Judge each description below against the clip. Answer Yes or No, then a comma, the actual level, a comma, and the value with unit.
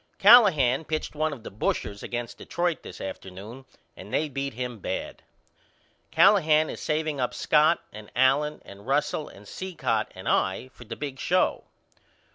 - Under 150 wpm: No, average, 155 wpm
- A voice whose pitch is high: No, low, 135 Hz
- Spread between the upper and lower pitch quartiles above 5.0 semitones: Yes, wide, 5.4 semitones